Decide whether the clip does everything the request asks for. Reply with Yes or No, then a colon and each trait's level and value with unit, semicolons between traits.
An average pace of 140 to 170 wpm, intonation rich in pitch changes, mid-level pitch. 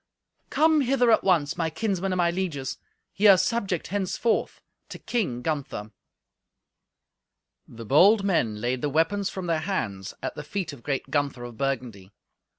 Yes: average, 155 wpm; wide, 6.9 semitones; medium, 165 Hz